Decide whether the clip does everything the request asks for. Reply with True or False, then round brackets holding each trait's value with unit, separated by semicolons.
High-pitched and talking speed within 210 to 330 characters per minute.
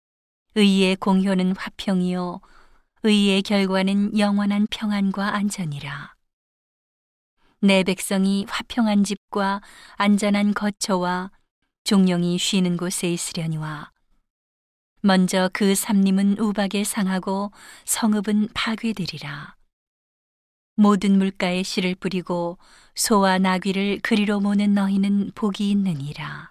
True (195 Hz; 225 characters per minute)